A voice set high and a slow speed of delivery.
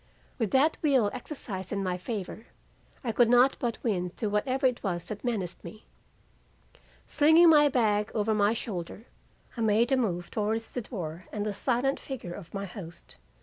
No: high, 215 Hz; average, 175 wpm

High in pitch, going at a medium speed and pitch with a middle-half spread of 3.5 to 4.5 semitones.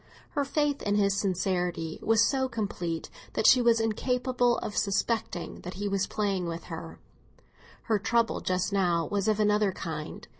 Yes: high, 205 Hz; average, 160 wpm; average, 4.2 semitones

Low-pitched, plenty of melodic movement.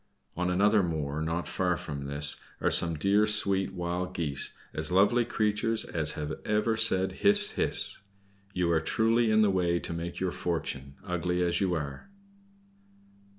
No: very low, 90 Hz; average, 4.5 semitones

